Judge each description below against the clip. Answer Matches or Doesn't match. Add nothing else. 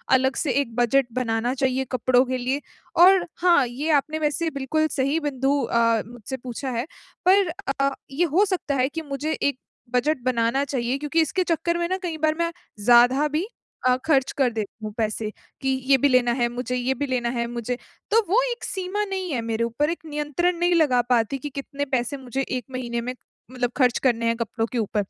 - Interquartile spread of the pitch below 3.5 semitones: Doesn't match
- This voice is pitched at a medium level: Doesn't match